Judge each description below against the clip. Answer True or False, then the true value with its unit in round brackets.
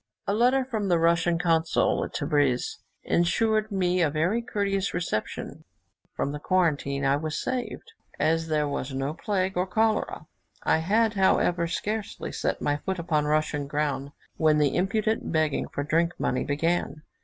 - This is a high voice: False (170 Hz)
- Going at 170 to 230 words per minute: False (155 wpm)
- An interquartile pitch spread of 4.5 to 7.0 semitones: True (4.8 semitones)